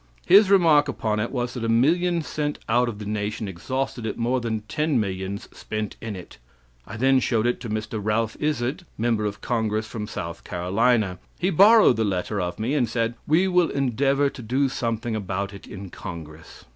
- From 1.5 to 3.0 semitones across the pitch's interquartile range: No, average, 4.4 semitones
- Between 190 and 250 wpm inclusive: Yes, average, 195 wpm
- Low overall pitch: Yes, low, 115 Hz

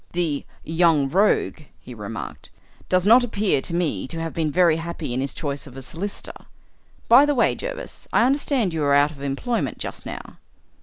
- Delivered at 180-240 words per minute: Yes, average, 190 wpm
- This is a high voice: No, medium, 170 Hz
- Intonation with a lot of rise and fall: Yes, wide, 6.7 semitones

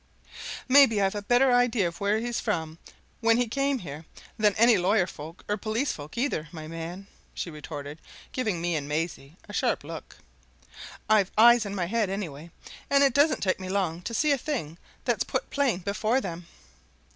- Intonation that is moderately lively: No, wide, 6.2 semitones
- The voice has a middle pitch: No, high, 200 Hz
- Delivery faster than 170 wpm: Yes, average, 190 wpm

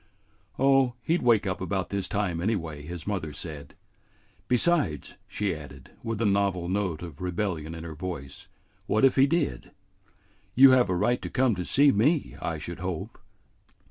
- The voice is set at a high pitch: No, very low, 95 Hz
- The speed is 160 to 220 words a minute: Yes, average, 175 wpm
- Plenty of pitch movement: Yes, wide, 6.5 semitones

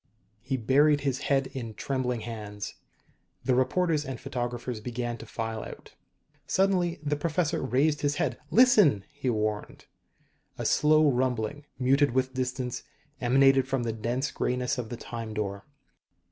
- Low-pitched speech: Yes, low, 130 Hz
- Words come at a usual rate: Yes, average, 145 wpm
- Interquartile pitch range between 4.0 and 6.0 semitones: No, average, 3.5 semitones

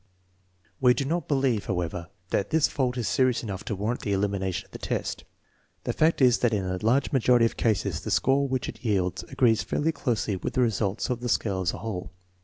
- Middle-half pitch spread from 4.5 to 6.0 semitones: Yes, average, 4.9 semitones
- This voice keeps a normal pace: No, fast, 215 wpm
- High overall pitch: No, low, 115 Hz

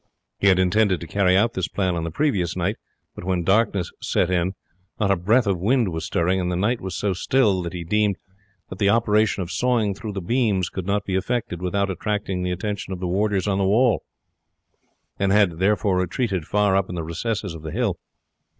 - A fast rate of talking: Yes, fast, 215 wpm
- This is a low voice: Yes, very low, 95 Hz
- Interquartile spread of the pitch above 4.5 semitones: No, narrow, 2.6 semitones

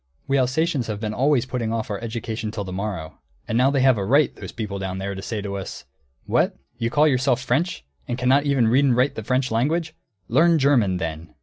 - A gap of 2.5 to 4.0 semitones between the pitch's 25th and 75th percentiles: No, average, 4.7 semitones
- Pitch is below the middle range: Yes, low, 120 Hz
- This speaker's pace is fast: Yes, fast, 225 wpm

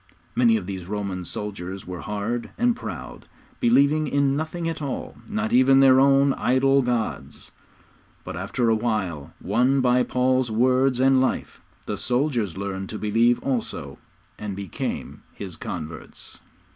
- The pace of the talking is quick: No, average, 145 wpm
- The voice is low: Yes, low, 120 Hz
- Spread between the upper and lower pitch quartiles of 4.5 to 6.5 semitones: Yes, average, 5.0 semitones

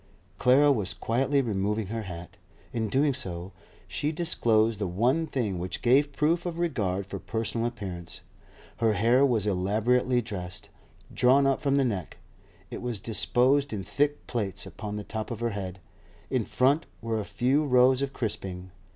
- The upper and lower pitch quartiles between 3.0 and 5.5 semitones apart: Yes, average, 5.0 semitones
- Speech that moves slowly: No, average, 165 wpm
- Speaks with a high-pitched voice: No, low, 115 Hz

